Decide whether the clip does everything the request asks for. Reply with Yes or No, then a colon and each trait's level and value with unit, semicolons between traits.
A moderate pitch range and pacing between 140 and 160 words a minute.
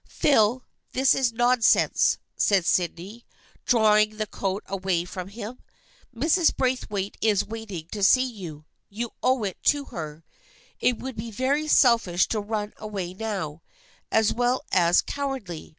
Yes: average, 4.6 semitones; average, 150 wpm